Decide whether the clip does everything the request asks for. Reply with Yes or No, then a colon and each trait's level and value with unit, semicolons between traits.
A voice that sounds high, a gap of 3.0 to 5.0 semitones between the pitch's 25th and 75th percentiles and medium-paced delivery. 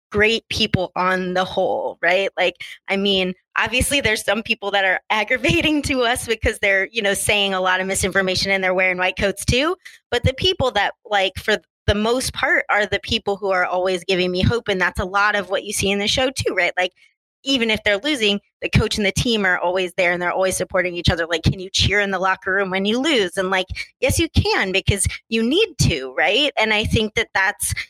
No: high, 200 Hz; average, 3.3 semitones; fast, 235 wpm